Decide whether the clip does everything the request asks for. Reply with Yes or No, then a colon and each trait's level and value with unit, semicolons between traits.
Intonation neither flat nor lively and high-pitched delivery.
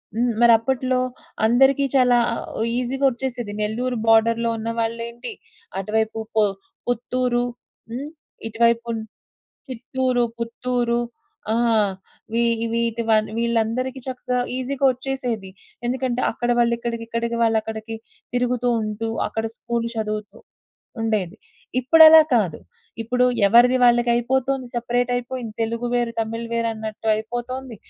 No: narrow, 1.8 semitones; high, 235 Hz